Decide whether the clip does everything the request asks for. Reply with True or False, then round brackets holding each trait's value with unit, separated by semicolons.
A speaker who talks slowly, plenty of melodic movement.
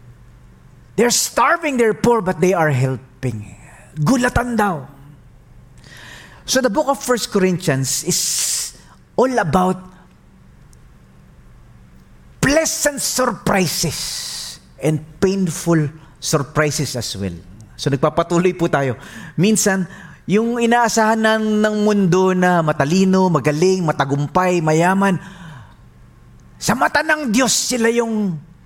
True (95 wpm; 7.2 semitones)